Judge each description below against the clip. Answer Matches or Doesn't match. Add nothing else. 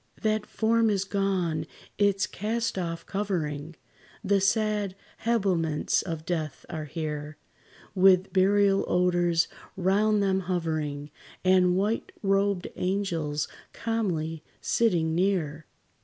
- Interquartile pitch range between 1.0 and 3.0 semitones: Doesn't match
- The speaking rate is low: Matches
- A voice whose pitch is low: Doesn't match